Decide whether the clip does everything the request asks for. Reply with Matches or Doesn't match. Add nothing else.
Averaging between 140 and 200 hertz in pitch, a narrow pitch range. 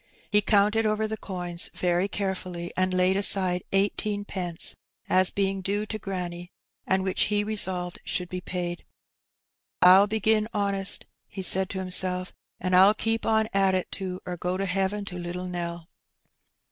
Matches